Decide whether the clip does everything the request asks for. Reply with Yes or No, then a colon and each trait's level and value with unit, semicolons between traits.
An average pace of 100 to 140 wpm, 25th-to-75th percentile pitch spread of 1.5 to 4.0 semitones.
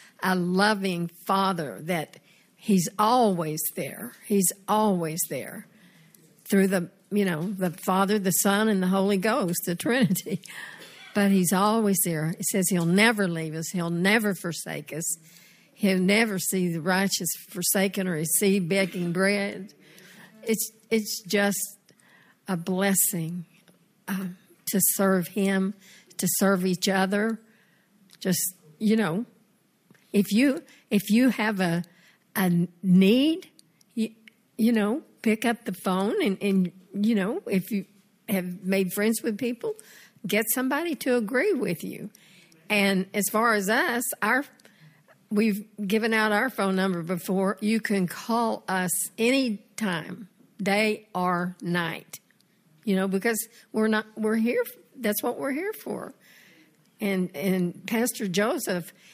Yes: slow, 135 wpm; average, 2.9 semitones